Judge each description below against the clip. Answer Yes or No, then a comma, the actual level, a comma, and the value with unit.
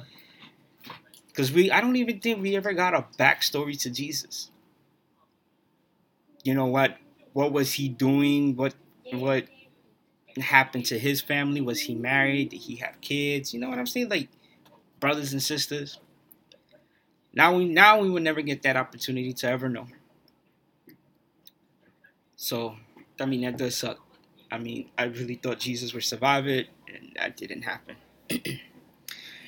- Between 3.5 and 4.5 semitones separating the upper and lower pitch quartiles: No, narrow, 2.4 semitones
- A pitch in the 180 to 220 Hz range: No, low, 135 Hz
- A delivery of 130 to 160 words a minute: Yes, average, 150 wpm